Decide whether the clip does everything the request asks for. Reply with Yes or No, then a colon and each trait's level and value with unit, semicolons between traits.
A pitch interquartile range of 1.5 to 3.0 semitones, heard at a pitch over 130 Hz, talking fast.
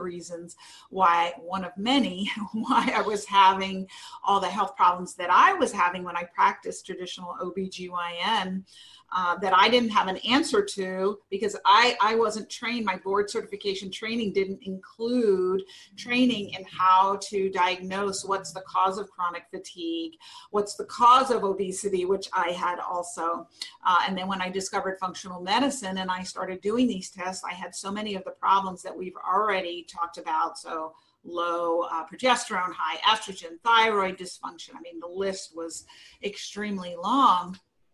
No: narrow, 2.6 semitones; high, 190 Hz; average, 160 wpm